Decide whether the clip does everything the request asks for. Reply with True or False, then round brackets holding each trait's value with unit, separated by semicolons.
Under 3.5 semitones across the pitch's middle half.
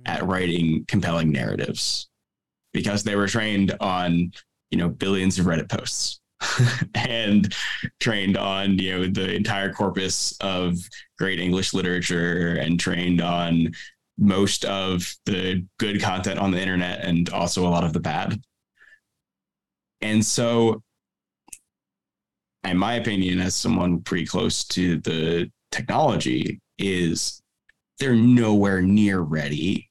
True (2.7 semitones)